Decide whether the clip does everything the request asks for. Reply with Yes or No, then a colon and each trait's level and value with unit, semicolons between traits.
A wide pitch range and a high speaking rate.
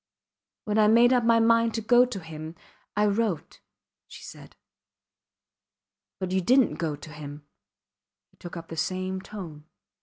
No: wide, 6.0 semitones; average, 160 wpm